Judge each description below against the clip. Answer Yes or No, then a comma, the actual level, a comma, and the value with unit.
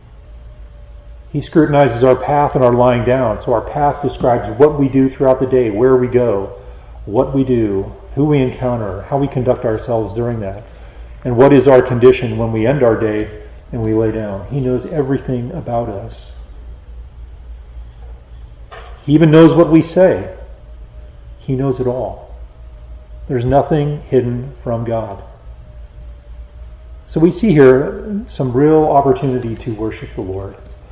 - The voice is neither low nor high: No, low, 120 Hz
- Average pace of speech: Yes, average, 150 wpm